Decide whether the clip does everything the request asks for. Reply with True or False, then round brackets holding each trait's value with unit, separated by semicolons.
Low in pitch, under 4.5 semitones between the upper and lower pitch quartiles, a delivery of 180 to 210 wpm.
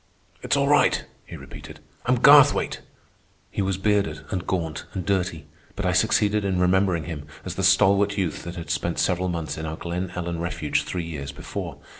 True (90 Hz; 2.8 semitones; 185 wpm)